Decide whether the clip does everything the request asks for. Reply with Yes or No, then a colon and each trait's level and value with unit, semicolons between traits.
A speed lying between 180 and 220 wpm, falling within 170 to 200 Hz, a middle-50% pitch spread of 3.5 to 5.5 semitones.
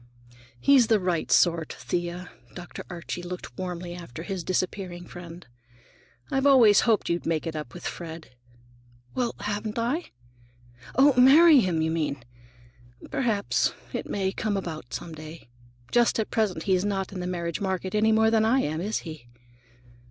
No: average, 160 wpm; medium, 185 Hz; average, 4.5 semitones